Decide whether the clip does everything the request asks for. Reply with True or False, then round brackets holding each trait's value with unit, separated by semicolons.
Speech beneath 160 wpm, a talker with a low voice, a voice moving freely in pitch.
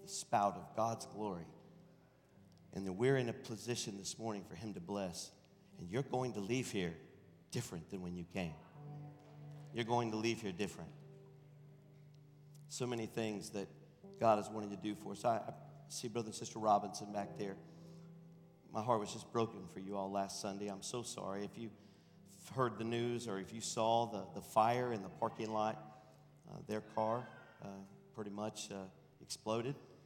False (180 wpm; 115 Hz; 5.8 semitones)